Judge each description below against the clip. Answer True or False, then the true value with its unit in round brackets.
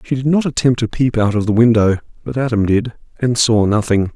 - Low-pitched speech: True (115 Hz)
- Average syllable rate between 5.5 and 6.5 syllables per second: True (5.6 syllables/s)